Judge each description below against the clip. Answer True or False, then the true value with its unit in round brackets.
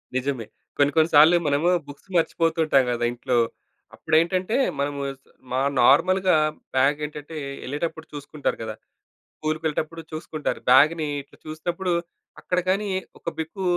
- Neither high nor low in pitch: True (155 Hz)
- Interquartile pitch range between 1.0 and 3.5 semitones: True (2.9 semitones)